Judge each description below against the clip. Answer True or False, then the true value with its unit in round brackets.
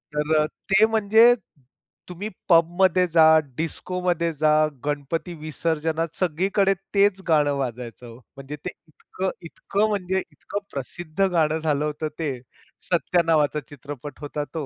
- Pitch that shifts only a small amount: False (3.6 semitones)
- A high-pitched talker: False (165 Hz)